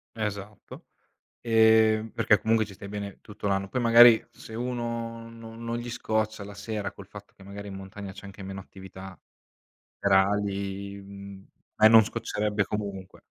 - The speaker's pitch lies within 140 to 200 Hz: No, low, 105 Hz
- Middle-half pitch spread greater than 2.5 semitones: No, narrow, 2.2 semitones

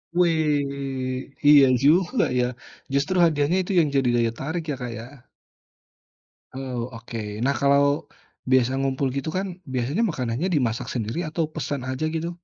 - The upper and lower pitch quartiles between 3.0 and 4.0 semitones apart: Yes, average, 3.7 semitones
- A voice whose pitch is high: No, medium, 140 Hz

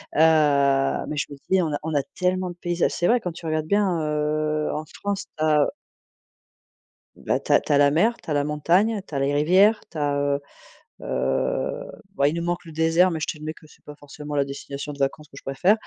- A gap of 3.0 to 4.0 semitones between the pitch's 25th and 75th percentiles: Yes, average, 3.3 semitones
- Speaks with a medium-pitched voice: Yes, medium, 155 Hz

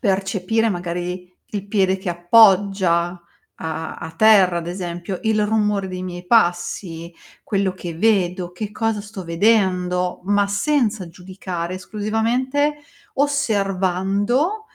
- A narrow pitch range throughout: No, average, 3.3 semitones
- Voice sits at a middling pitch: No, high, 195 Hz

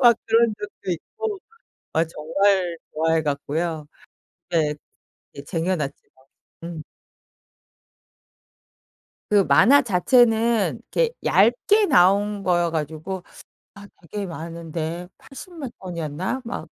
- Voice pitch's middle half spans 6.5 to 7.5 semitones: No, wide, 5.6 semitones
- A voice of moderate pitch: Yes, medium, 180 Hz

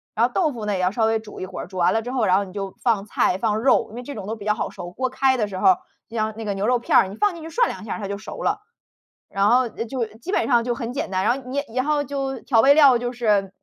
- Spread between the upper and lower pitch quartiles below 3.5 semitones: No, average, 4.2 semitones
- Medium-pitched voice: No, high, 225 Hz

